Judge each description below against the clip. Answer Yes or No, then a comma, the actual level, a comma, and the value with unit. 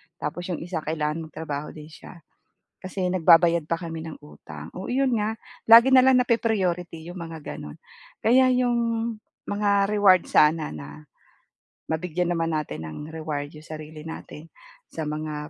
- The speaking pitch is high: No, medium, 165 Hz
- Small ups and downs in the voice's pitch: No, average, 3.6 semitones